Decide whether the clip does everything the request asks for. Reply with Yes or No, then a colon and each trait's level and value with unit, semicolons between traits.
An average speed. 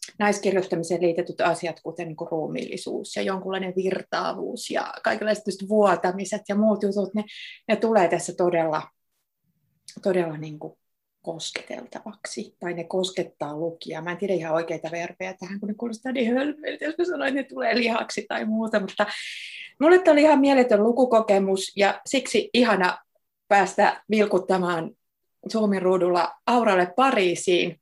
Yes: average, 140 wpm